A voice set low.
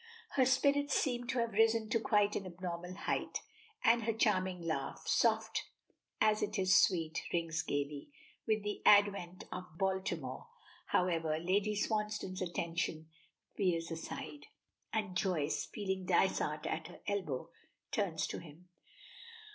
No: medium, 185 Hz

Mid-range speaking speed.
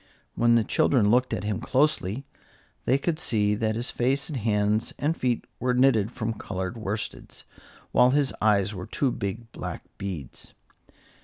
Yes: average, 160 wpm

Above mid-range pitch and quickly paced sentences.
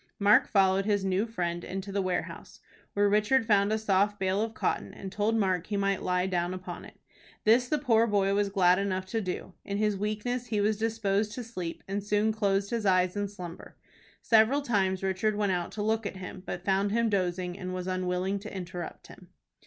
Yes: high, 200 Hz; fast, 210 wpm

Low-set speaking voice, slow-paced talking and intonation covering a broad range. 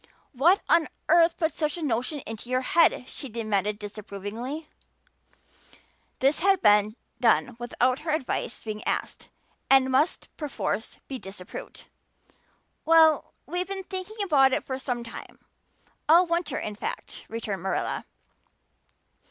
No: very high, 260 Hz; slow, 130 wpm; wide, 6.5 semitones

